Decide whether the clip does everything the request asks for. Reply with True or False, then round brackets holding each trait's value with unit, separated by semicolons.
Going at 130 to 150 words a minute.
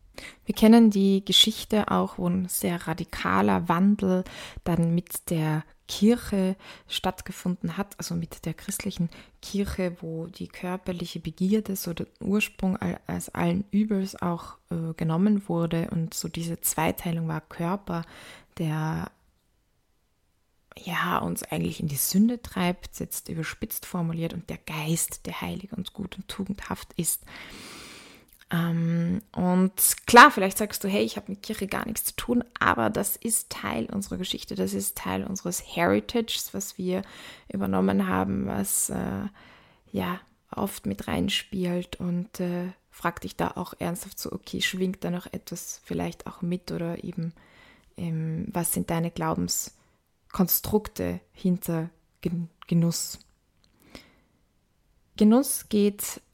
True (135 wpm)